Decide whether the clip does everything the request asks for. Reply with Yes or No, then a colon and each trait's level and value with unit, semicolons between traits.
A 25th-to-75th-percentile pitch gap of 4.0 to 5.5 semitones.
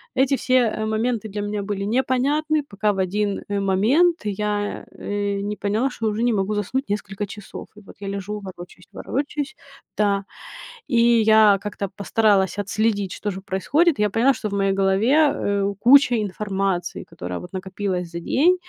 No: average, 3.0 semitones